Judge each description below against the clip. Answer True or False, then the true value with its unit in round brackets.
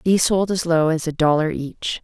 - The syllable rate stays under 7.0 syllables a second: True (5.2 syllables/s)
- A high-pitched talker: False (165 Hz)